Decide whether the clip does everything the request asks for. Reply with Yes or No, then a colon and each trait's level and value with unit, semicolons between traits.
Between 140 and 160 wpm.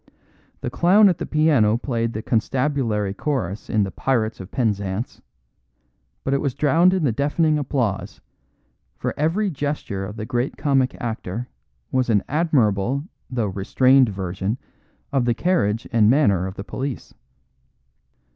Yes: average, 145 wpm